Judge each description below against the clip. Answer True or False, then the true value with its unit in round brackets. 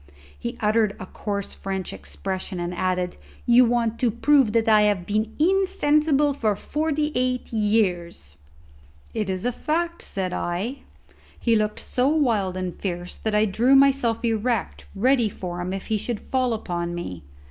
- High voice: True (220 Hz)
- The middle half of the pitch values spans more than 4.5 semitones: True (5.1 semitones)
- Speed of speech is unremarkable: True (160 wpm)